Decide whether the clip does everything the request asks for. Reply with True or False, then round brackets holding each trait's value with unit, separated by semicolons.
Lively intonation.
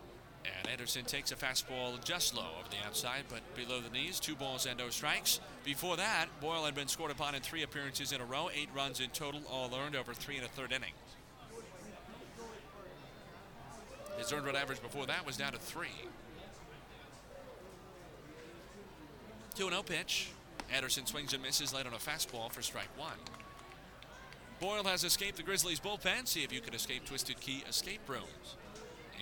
False (3.6 semitones)